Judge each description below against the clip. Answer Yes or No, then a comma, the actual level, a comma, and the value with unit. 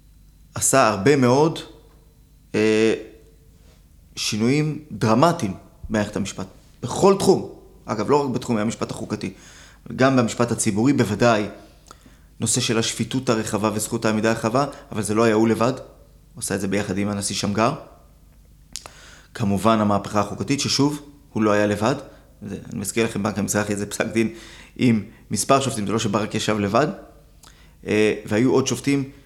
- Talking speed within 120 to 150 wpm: Yes, average, 140 wpm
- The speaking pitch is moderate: No, low, 110 Hz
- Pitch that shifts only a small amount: No, average, 3.4 semitones